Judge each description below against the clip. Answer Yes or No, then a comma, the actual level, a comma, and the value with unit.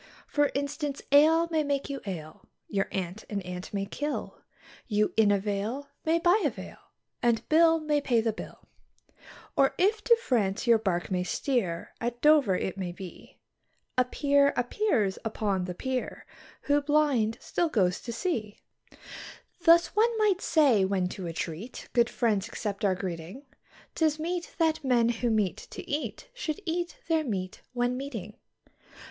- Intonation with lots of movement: Yes, wide, 7.3 semitones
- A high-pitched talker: Yes, high, 245 Hz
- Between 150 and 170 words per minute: Yes, average, 165 wpm